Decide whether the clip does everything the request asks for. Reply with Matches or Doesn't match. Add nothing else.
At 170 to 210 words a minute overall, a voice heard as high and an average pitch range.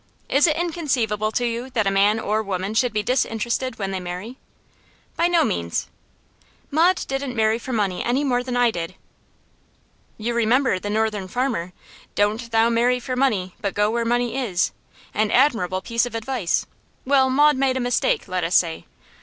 Matches